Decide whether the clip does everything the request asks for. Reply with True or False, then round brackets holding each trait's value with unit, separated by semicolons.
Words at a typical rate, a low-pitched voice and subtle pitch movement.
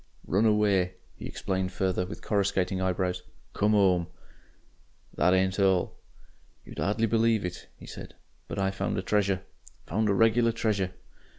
True (150 wpm; 95 Hz; 2.3 semitones)